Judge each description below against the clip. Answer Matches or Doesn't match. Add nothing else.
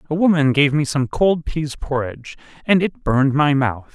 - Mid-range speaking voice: Matches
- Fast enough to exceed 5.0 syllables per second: Matches